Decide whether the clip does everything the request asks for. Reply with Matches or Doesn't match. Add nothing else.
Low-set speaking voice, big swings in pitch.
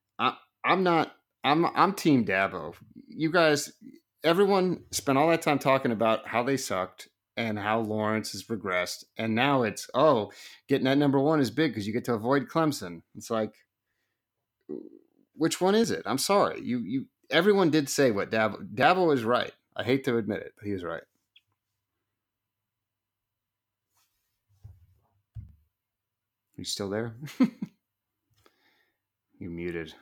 Matches